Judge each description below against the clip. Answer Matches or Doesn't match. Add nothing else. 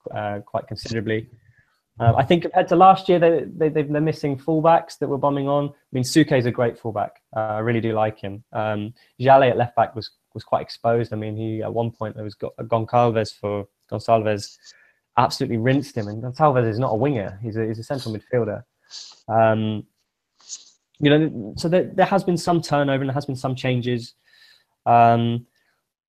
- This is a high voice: Doesn't match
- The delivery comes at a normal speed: Matches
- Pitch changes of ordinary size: Matches